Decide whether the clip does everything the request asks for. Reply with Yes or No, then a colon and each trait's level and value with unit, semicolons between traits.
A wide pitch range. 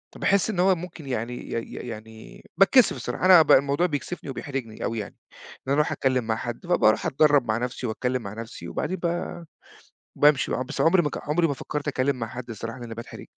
Yes: wide, 6.0 semitones